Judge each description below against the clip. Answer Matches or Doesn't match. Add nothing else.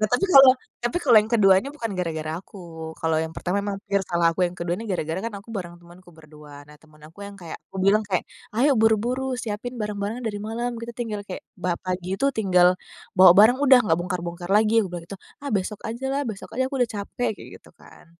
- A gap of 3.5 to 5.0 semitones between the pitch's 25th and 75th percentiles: Matches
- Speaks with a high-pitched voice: Matches